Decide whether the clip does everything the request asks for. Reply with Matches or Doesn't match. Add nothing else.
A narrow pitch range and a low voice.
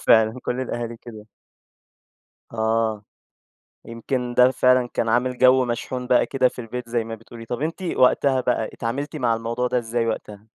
Matches